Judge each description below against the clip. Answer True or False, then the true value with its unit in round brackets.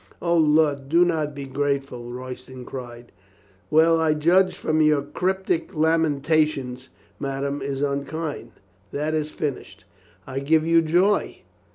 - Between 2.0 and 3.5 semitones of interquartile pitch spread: True (2.8 semitones)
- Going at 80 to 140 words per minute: True (135 wpm)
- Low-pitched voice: False (150 Hz)